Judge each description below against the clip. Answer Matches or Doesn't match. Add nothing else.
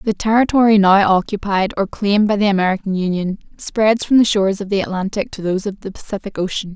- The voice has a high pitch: Matches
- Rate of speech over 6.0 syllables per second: Matches